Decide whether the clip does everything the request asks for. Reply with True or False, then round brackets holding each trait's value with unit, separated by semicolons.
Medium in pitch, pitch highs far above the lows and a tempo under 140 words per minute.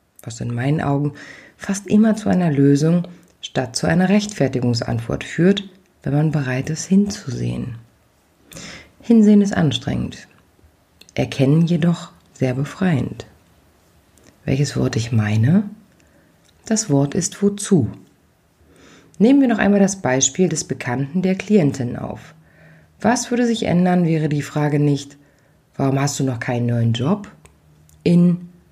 True (145 Hz; 7.6 semitones; 125 wpm)